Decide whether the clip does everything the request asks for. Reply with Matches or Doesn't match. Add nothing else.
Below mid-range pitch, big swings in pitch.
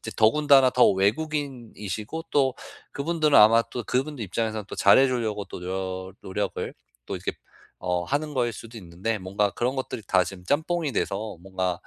Matches